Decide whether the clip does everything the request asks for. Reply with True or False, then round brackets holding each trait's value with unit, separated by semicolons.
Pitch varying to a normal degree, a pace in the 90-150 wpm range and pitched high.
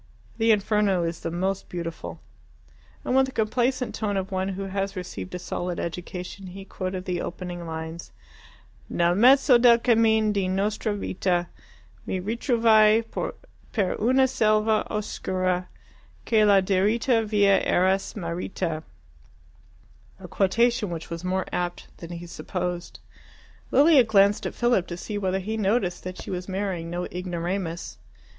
True (3.4 semitones; 140 wpm; 195 Hz)